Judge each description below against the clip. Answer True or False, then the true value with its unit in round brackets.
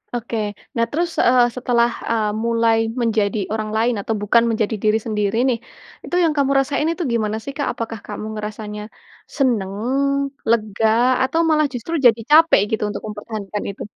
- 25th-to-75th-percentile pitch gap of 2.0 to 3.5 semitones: True (2.8 semitones)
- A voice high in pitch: True (230 Hz)